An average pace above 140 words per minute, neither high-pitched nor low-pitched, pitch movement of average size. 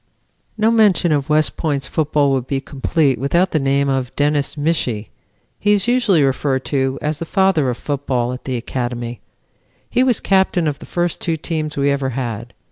Yes: average, 185 wpm; medium, 145 Hz; average, 4.0 semitones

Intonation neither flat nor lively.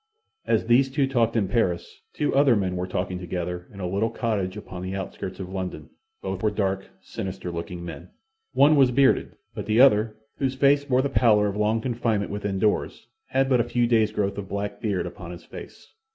Yes: average, 4.4 semitones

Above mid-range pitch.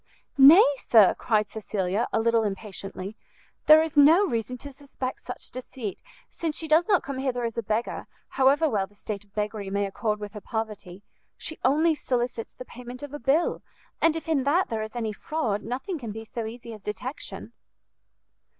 Yes: high, 235 Hz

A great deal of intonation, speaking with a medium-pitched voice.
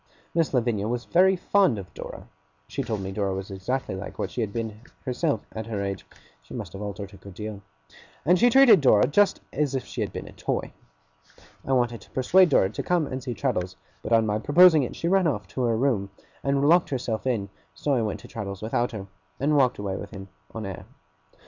No: wide, 6.0 semitones; low, 115 Hz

